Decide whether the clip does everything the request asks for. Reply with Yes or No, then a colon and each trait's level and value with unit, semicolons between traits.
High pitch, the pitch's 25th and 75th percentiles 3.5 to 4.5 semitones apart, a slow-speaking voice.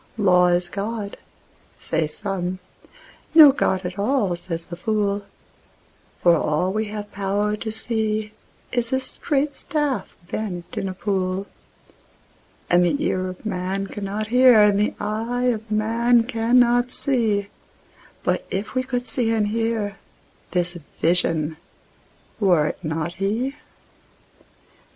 Yes: high, 205 Hz; average, 3.9 semitones; slow, 120 wpm